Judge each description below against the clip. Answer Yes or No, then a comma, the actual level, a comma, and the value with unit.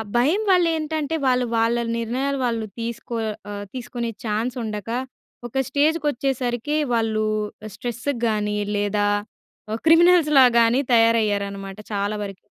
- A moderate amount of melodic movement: Yes, average, 4.1 semitones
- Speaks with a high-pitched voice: Yes, high, 235 Hz